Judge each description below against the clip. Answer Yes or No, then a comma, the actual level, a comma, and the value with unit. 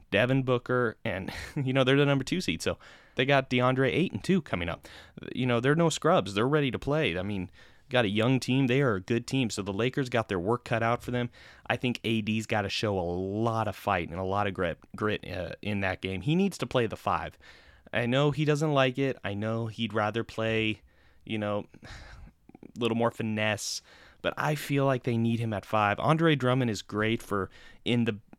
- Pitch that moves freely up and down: No, average, 4.3 semitones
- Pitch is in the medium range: No, low, 115 Hz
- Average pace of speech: No, fast, 230 wpm